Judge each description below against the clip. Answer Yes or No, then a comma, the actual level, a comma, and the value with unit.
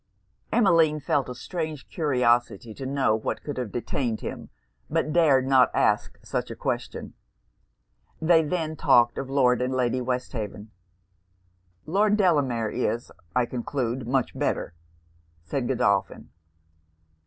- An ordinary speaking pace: No, slow, 125 wpm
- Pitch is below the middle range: Yes, low, 130 Hz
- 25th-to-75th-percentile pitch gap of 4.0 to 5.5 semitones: Yes, average, 4.3 semitones